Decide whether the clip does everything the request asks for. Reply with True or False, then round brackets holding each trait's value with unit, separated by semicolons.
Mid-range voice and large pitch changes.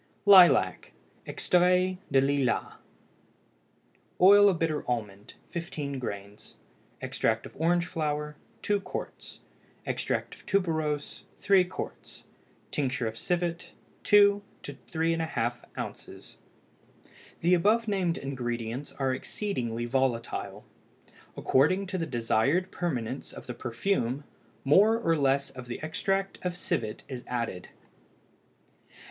True (150 Hz; 6.5 semitones)